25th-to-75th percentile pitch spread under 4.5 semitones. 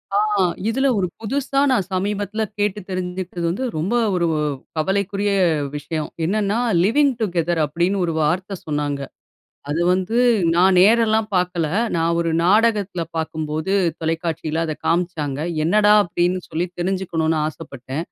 Yes: average, 3.8 semitones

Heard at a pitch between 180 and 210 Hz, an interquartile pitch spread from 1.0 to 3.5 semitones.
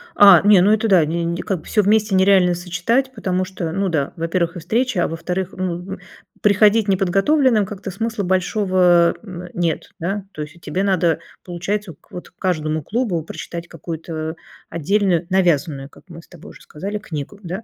Yes: medium, 185 Hz; average, 3.1 semitones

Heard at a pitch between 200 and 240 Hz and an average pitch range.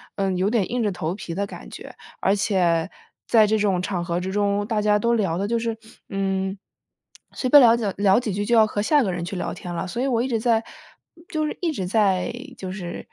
Yes: high, 205 Hz; average, 3.4 semitones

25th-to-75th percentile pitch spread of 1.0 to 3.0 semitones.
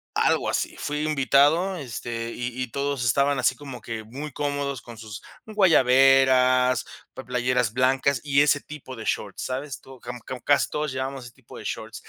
Yes: narrow, 2.6 semitones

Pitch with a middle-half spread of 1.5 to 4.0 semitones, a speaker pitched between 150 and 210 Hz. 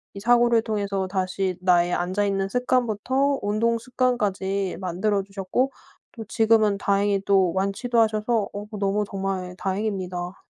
Yes: average, 2.8 semitones; high, 200 Hz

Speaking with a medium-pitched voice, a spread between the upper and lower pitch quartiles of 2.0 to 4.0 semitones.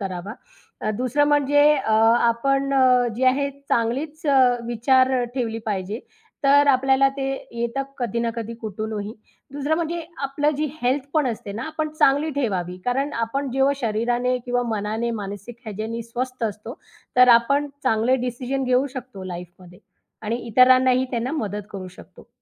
No: high, 245 Hz; average, 3.6 semitones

